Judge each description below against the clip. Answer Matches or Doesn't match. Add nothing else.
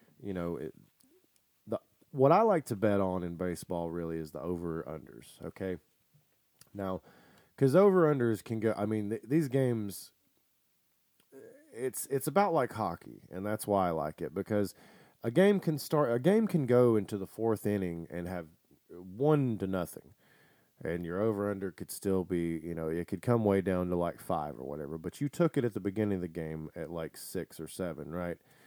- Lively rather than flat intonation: Matches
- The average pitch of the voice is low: Matches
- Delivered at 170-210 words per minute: Matches